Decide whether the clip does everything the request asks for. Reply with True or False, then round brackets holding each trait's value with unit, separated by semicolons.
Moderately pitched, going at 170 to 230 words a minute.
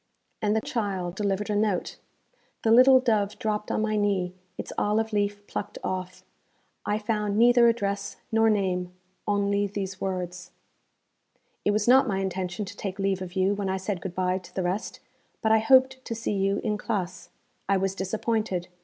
False (205 Hz; 180 wpm)